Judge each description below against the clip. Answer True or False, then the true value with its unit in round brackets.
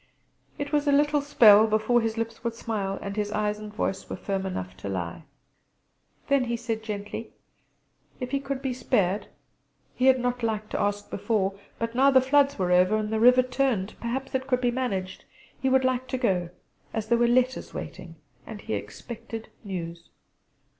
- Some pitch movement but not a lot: True (4.1 semitones)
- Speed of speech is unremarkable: True (185 wpm)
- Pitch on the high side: True (225 Hz)